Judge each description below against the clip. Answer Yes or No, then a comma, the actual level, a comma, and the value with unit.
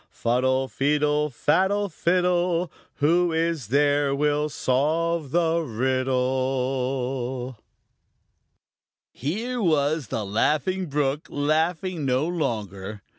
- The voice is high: No, medium, 145 Hz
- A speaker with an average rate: No, slow, 85 wpm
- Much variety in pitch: No, average, 4.3 semitones